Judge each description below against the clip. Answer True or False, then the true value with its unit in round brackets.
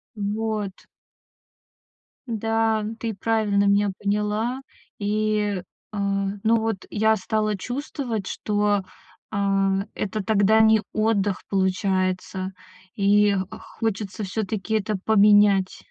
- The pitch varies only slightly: True (1.7 semitones)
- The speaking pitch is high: True (210 Hz)